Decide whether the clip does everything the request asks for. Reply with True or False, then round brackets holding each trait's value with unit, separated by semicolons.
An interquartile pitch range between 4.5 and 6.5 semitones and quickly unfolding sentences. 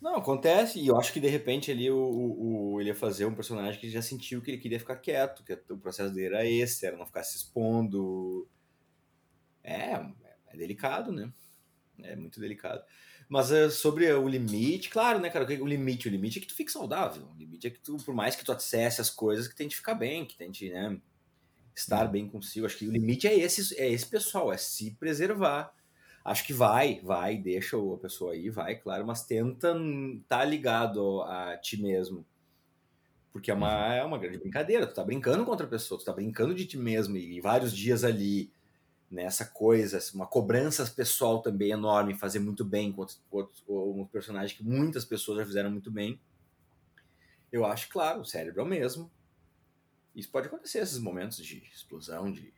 True (5.0 semitones; 205 wpm)